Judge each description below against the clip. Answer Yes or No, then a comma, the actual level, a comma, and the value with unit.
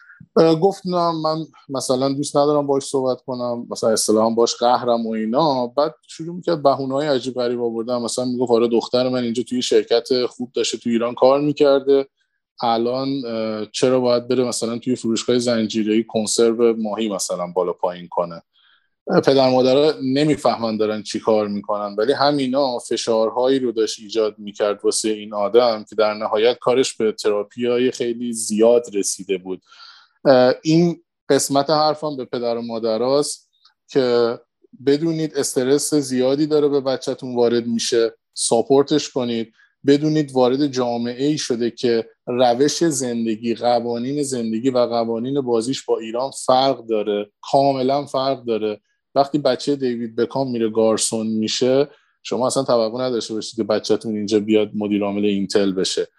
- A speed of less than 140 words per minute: No, average, 145 wpm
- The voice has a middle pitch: No, low, 120 Hz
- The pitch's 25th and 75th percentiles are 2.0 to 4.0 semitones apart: Yes, average, 3.6 semitones